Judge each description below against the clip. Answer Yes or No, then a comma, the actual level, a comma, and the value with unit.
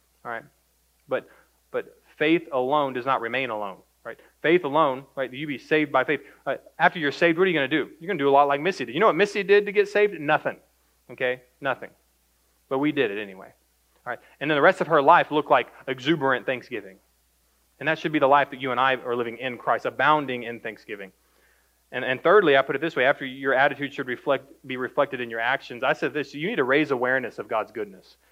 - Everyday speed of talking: No, fast, 240 wpm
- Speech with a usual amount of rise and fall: Yes, average, 3.8 semitones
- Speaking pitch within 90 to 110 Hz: No, low, 135 Hz